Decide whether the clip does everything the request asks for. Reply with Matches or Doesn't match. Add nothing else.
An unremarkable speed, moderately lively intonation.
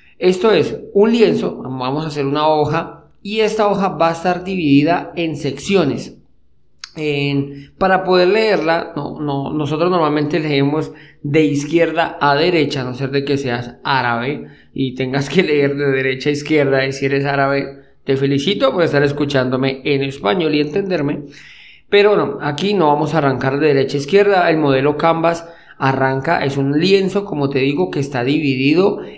Matches